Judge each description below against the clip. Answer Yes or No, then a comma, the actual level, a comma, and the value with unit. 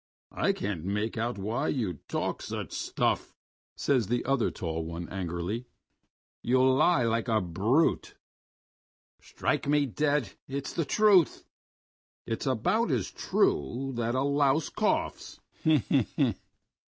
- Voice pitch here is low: Yes, low, 120 Hz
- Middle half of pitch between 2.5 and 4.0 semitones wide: No, wide, 5.5 semitones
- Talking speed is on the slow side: Yes, slow, 125 wpm